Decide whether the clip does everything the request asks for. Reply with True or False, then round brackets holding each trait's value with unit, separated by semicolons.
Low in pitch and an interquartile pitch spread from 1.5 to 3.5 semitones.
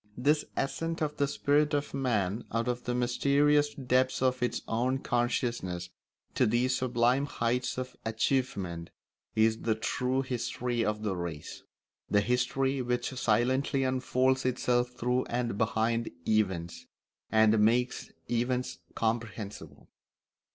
True (125 Hz; 2.6 semitones)